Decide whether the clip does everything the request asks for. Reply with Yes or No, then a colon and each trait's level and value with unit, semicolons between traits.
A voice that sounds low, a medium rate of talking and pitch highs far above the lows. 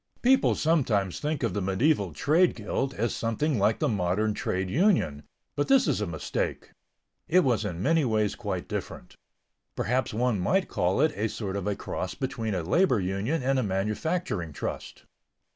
Yes: low, 110 Hz; average, 180 wpm; wide, 7.0 semitones